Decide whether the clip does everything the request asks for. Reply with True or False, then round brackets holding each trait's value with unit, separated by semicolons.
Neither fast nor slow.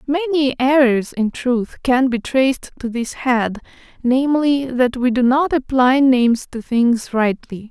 True (155 wpm)